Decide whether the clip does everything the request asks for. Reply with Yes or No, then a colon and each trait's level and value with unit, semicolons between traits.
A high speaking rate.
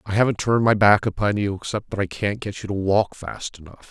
Yes: fast, 260 wpm